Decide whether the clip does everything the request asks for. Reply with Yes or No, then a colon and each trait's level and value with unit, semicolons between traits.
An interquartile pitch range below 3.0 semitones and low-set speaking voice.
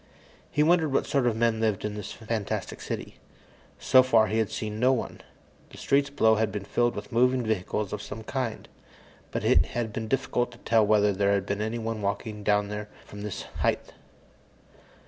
Yes: narrow, 2.5 semitones; low, 110 Hz